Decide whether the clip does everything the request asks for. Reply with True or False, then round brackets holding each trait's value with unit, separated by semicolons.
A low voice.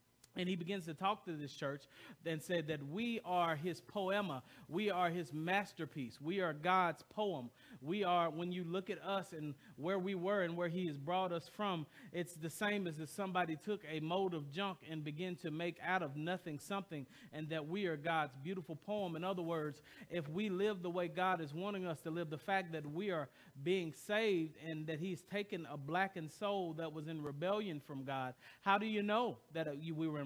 False (175 Hz)